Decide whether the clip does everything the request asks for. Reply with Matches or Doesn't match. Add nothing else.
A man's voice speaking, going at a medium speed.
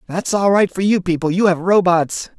Doesn't match